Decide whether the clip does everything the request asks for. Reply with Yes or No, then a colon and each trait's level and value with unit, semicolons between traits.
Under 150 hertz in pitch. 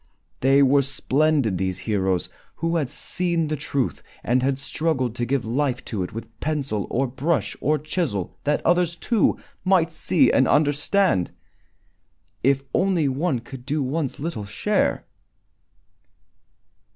Yes: medium, 140 Hz